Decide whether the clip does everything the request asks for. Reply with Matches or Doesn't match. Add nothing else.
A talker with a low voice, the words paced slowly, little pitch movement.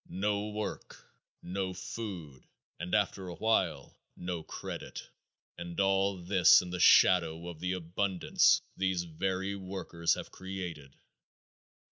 Matches